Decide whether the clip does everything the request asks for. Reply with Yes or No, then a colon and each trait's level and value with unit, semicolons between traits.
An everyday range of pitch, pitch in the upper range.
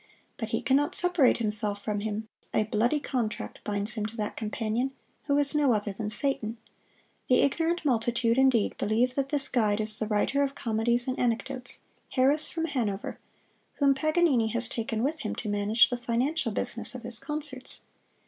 Yes: average, 4.2 semitones; high, 240 Hz